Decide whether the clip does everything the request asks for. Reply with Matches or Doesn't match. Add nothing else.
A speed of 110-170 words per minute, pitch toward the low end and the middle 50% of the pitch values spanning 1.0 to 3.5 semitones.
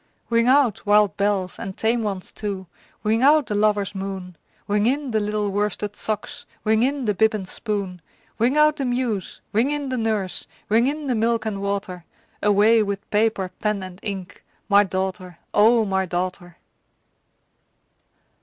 Doesn't match